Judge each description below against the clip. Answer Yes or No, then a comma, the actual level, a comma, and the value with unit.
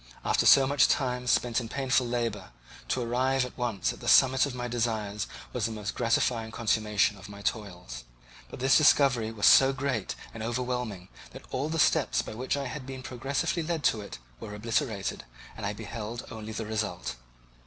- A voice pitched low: Yes, low, 120 Hz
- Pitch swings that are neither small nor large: Yes, average, 3.5 semitones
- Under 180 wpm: No, average, 185 wpm